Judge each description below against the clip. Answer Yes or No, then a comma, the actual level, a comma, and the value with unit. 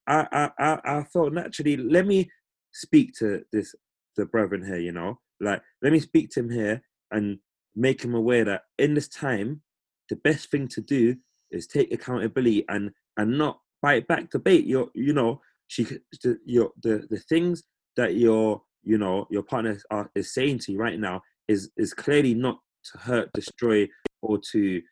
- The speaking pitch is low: Yes, low, 120 Hz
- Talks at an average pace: Yes, average, 185 wpm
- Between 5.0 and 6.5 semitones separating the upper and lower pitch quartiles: Yes, wide, 5.5 semitones